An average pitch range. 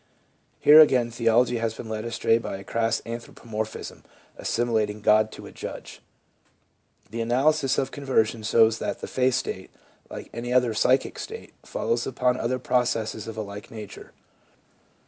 No: narrow, 2.2 semitones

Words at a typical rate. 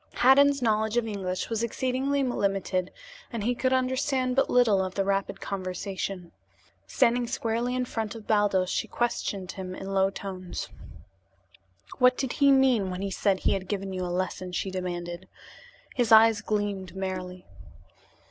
Yes: average, 155 wpm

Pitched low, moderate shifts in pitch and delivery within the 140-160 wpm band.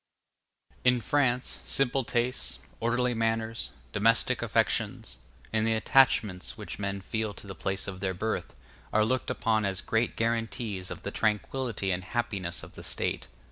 Yes: low, 110 Hz; average, 3.3 semitones; average, 150 wpm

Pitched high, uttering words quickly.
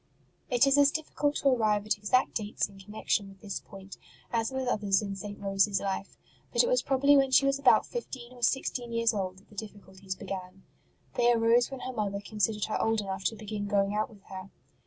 Yes: high, 215 Hz; fast, 220 wpm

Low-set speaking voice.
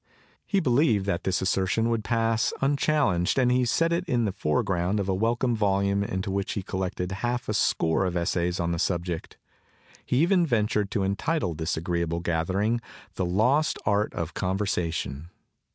Yes: low, 100 Hz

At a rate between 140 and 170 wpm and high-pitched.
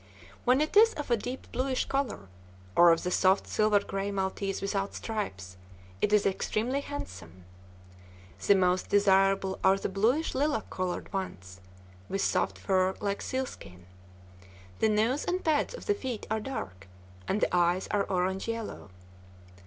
Yes: average, 155 wpm; high, 200 Hz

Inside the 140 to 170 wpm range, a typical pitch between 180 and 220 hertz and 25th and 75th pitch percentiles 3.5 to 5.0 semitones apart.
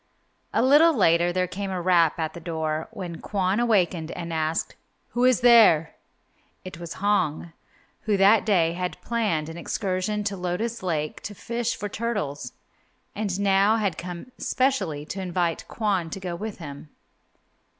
Yes: average, 160 wpm; medium, 185 Hz; average, 4.0 semitones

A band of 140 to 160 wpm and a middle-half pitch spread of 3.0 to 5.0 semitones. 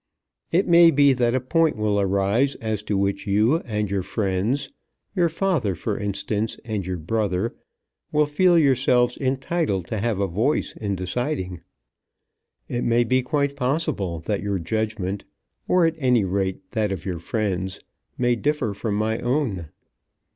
No: average, 155 wpm; wide, 5.5 semitones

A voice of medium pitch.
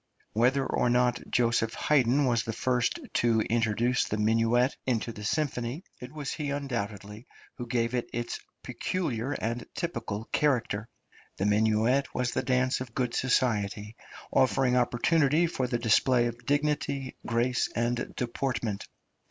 No: low, 120 Hz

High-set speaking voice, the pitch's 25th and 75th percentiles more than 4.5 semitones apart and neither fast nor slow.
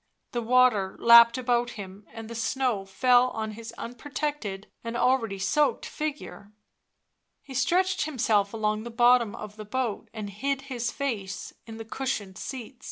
No: high, 235 Hz; average, 3.3 semitones; average, 155 wpm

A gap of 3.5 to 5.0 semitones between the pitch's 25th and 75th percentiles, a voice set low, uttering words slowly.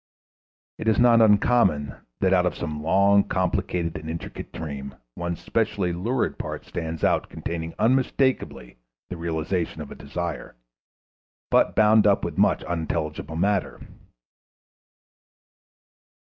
Yes: average, 4.0 semitones; very low, 85 Hz; slow, 120 wpm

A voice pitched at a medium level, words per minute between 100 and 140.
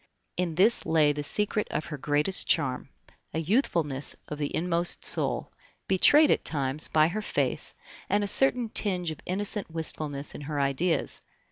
No: medium, 165 Hz; average, 160 wpm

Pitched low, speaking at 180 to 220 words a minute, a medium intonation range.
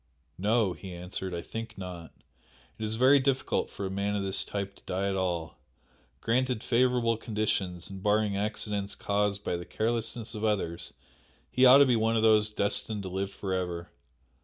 Yes: low, 105 Hz; average, 185 wpm; average, 3.1 semitones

